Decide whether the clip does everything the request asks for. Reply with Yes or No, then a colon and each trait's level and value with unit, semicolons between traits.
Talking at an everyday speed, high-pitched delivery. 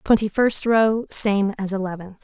Yes: average, 160 wpm; high, 205 Hz